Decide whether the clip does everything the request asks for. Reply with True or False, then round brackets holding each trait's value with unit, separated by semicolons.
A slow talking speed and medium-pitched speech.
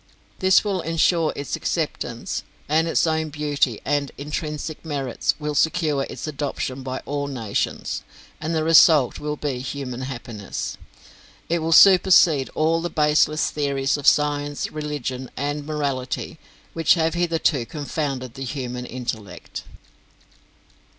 True (130 wpm; 145 Hz)